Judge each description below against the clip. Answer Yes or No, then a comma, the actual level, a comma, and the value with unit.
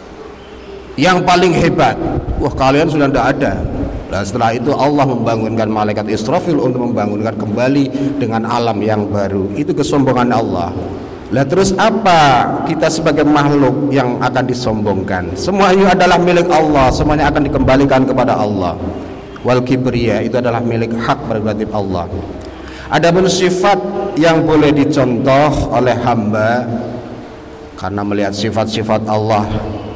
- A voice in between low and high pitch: No, low, 125 Hz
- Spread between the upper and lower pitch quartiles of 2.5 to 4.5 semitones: No, average, 5.3 semitones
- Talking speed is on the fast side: No, average, 125 wpm